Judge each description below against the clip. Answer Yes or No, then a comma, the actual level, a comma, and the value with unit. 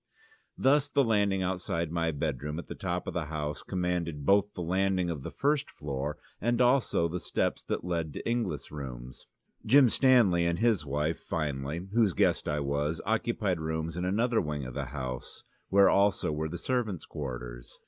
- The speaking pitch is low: Yes, very low, 85 Hz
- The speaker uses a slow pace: No, average, 180 wpm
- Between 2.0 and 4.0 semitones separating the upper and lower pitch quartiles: No, wide, 5.4 semitones